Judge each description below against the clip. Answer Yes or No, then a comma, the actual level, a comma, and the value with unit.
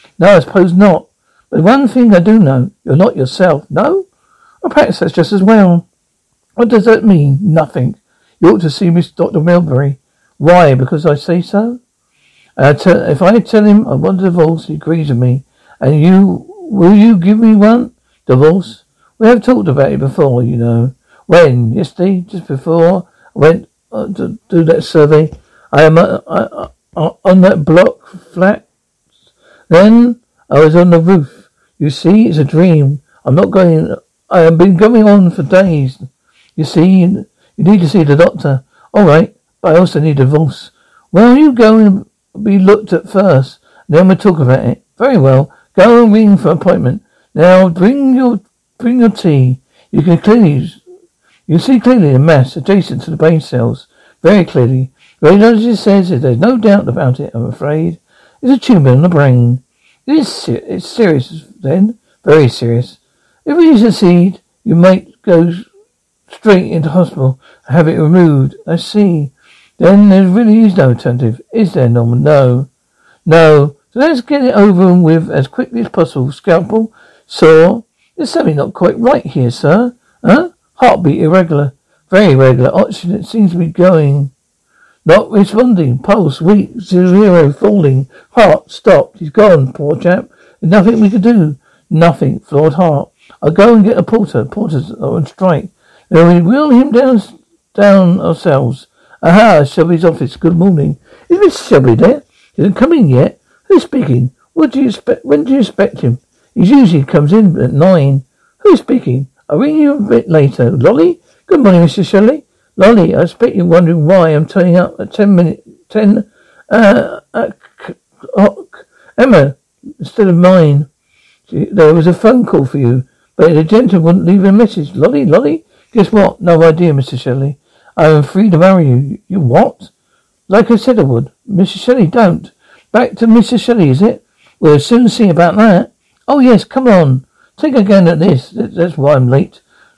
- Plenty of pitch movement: Yes, wide, 6.2 semitones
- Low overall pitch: No, medium, 180 Hz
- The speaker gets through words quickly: No, average, 175 wpm